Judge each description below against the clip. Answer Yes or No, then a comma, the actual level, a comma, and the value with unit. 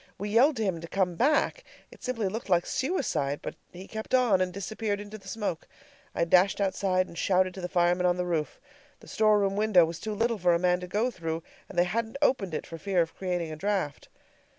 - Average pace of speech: No, fast, 230 wpm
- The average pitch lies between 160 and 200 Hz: Yes, high, 190 Hz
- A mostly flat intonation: No, average, 3.6 semitones